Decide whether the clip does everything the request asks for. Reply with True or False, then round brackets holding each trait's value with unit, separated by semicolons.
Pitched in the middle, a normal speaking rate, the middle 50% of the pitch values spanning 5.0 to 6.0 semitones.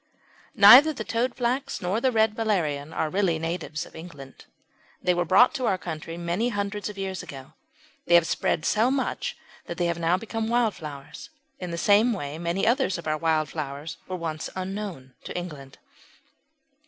True (180 Hz; 175 wpm; 5.3 semitones)